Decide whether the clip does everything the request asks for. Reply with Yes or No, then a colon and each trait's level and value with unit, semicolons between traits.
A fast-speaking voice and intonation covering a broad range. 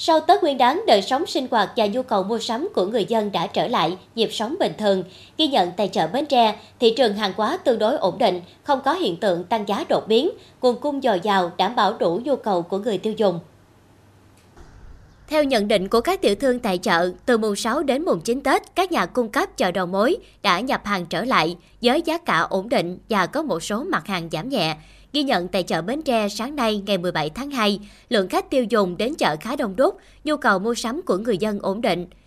No: average, 240 wpm; wide, 5.8 semitones